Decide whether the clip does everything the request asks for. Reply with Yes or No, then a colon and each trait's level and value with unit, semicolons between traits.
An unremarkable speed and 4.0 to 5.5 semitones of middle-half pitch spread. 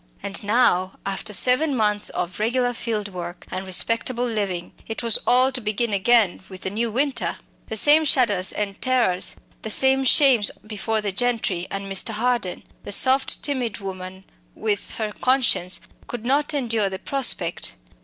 Yes: average, 160 wpm; average, 4.3 semitones